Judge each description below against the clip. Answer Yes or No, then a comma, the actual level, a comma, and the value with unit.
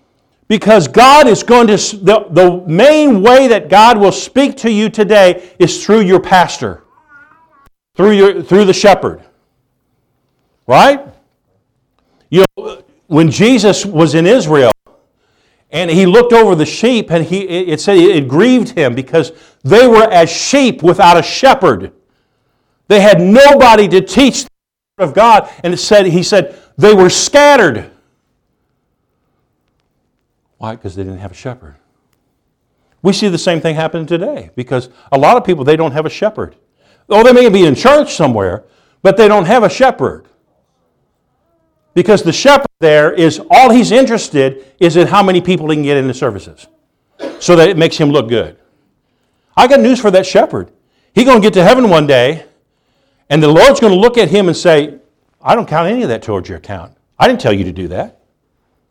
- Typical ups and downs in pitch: No, wide, 6.5 semitones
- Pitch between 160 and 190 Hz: Yes, medium, 185 Hz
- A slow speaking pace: No, average, 175 wpm